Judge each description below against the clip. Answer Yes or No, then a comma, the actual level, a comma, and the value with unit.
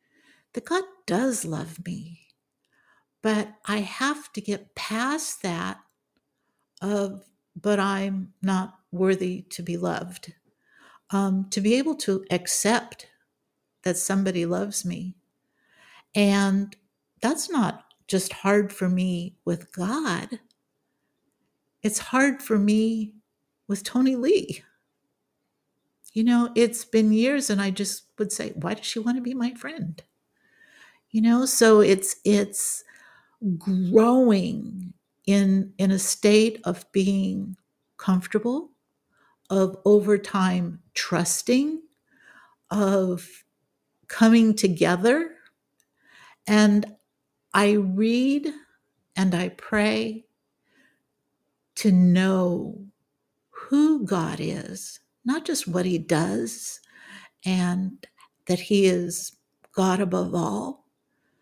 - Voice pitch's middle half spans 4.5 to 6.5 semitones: No, average, 3.6 semitones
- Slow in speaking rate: Yes, slow, 105 wpm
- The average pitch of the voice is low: No, high, 200 Hz